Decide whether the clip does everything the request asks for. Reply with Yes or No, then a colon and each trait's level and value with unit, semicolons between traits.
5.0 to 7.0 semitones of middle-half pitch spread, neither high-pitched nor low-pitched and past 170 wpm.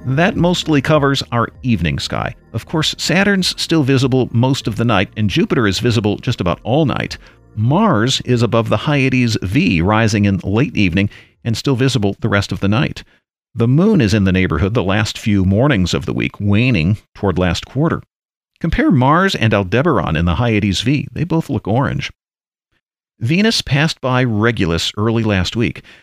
No: wide, 5.5 semitones; low, 115 Hz; average, 180 wpm